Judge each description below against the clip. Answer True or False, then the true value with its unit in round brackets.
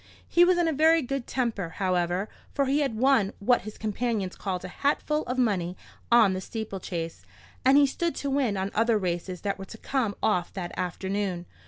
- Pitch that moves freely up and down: True (6.1 semitones)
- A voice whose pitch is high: True (215 Hz)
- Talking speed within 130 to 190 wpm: False (200 wpm)